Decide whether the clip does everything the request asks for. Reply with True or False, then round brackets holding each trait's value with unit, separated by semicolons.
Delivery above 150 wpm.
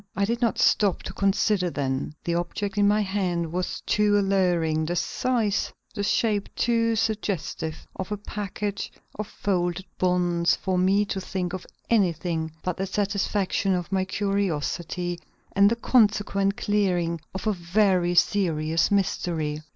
False (145 wpm)